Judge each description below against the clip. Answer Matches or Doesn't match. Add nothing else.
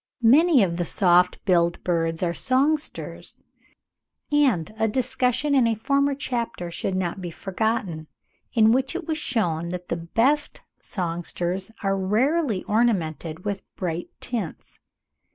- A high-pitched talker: Matches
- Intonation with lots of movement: Matches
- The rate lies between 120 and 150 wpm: Matches